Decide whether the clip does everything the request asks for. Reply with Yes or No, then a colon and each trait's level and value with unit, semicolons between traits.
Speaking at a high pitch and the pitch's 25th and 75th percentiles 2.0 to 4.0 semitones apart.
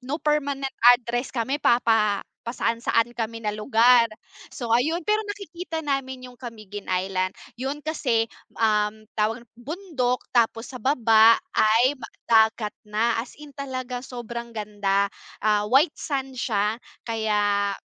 Yes: high, 235 Hz; average, 3.7 semitones